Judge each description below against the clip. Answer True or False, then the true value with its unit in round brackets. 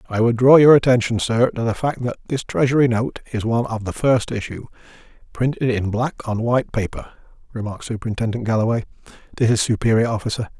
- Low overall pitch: True (115 Hz)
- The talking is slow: False (175 wpm)